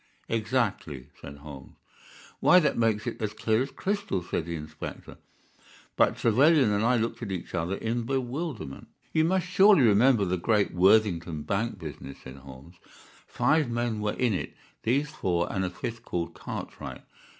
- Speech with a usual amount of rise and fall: No, wide, 6.5 semitones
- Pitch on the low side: Yes, low, 110 Hz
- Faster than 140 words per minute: Yes, average, 160 wpm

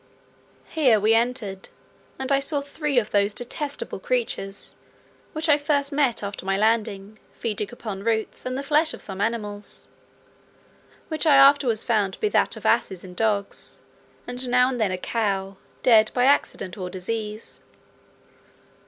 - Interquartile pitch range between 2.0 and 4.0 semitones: No, average, 5.2 semitones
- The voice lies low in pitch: No, high, 225 Hz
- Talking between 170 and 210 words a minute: No, average, 155 wpm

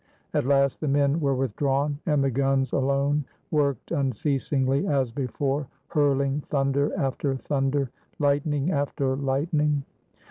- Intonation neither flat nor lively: No, narrow, 1.3 semitones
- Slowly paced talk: Yes, slow, 120 wpm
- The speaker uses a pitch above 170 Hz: No, medium, 140 Hz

